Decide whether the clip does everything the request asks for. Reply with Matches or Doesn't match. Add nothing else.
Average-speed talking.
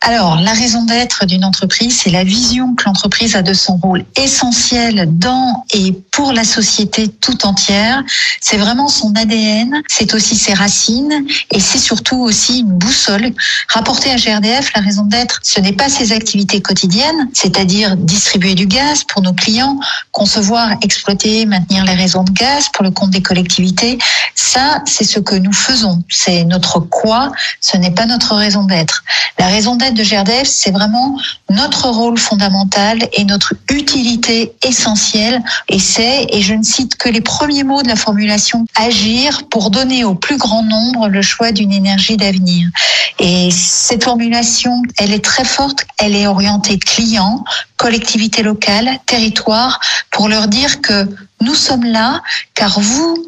Matches